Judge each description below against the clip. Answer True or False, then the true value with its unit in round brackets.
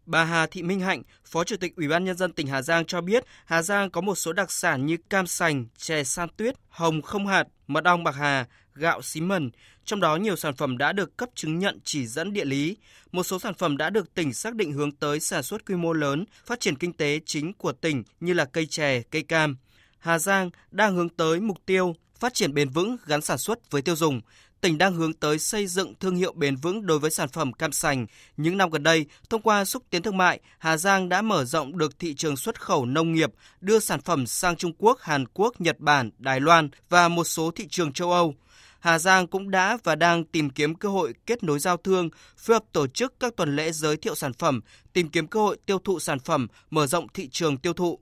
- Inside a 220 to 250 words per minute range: True (245 wpm)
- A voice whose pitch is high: False (165 Hz)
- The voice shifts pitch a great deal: False (3.9 semitones)